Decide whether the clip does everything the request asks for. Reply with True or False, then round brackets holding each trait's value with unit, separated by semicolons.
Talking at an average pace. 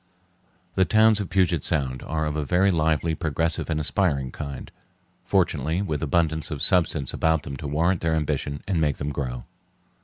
True (175 wpm)